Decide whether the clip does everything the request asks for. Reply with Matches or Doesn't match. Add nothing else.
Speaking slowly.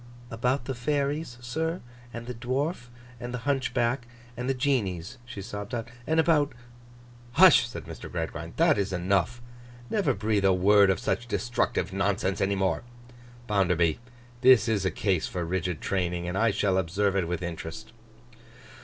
Doesn't match